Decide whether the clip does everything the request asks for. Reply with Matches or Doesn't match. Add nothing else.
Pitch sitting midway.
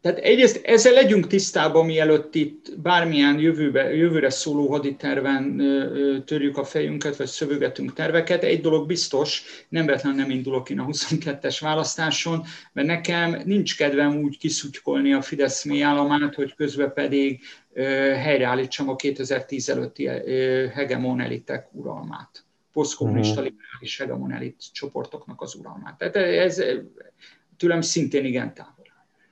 Matches